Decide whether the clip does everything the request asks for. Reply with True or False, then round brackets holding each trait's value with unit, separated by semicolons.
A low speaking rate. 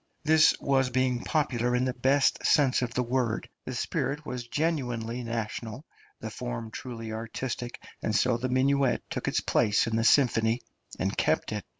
False (170 wpm)